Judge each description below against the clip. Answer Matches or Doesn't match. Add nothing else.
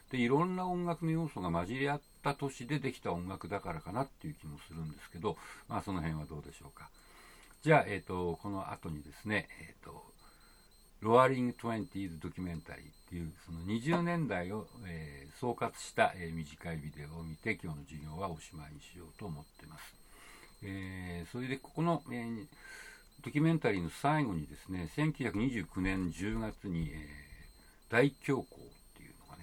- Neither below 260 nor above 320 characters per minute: Matches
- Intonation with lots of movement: Matches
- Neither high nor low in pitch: Doesn't match